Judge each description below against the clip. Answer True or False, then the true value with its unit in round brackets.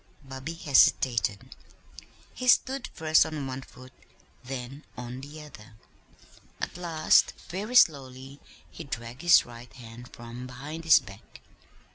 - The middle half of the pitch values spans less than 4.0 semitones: False (4.3 semitones)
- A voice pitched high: False (135 Hz)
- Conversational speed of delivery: False (125 wpm)